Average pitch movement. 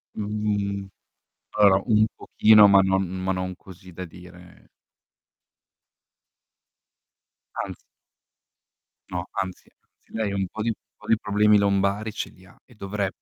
No: narrow, 2.2 semitones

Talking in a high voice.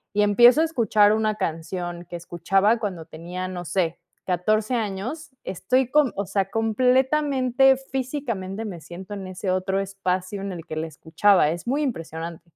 Yes: high, 195 Hz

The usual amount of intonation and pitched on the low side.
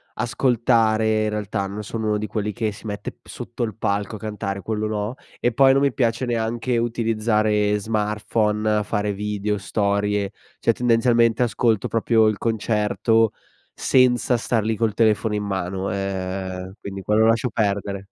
No: narrow, 1.9 semitones; low, 110 Hz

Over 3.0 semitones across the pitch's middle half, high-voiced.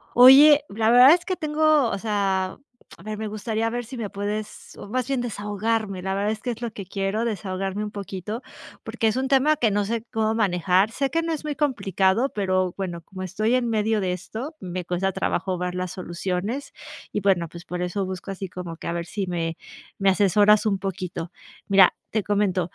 Yes: average, 3.5 semitones; high, 205 Hz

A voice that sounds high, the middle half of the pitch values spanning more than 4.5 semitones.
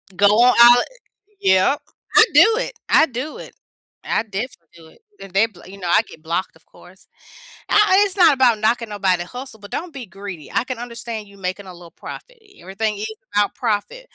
Yes: high, 215 Hz; average, 4.9 semitones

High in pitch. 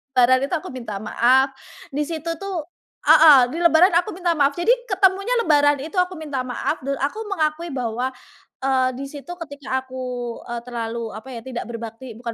Yes: very high, 275 Hz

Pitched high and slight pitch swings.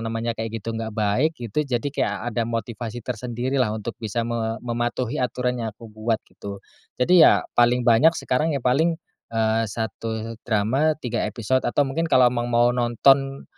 No: low, 120 Hz; narrow, 2.2 semitones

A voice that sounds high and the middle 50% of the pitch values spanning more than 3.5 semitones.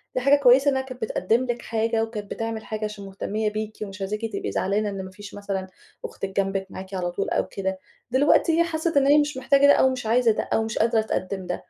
Yes: high, 220 Hz; average, 4.6 semitones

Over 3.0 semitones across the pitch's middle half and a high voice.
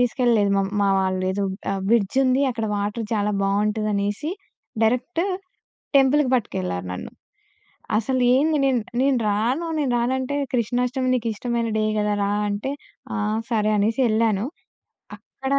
Yes: average, 3.8 semitones; high, 230 Hz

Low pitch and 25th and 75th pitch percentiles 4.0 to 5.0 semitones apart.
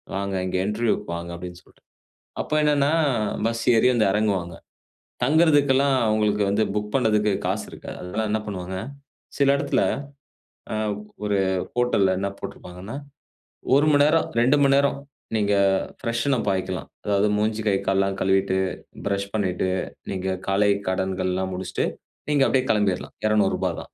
Yes: low, 105 Hz; average, 4.3 semitones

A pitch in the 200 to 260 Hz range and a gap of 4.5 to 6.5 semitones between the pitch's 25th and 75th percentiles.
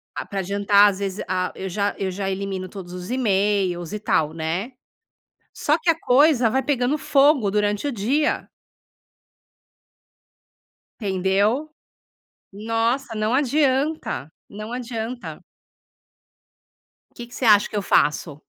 Yes: high, 210 Hz; average, 4.8 semitones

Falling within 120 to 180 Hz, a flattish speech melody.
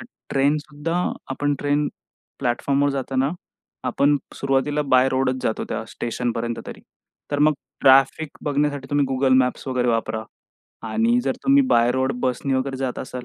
Yes: low, 135 Hz; narrow, 2.1 semitones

